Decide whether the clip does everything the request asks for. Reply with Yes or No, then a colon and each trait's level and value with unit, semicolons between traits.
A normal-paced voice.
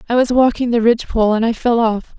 No: fast, 245 wpm